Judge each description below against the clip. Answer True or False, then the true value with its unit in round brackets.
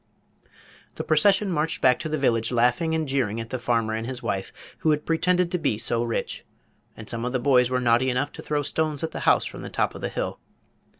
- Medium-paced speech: False (235 wpm)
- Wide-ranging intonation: False (4.8 semitones)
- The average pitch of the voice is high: False (130 Hz)